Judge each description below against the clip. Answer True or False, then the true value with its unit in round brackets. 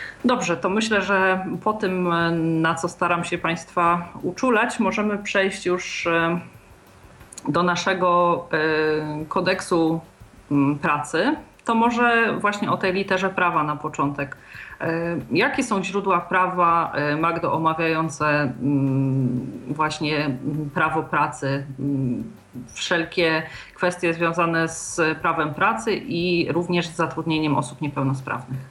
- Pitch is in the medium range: True (165 Hz)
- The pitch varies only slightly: False (3.6 semitones)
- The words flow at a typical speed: False (100 wpm)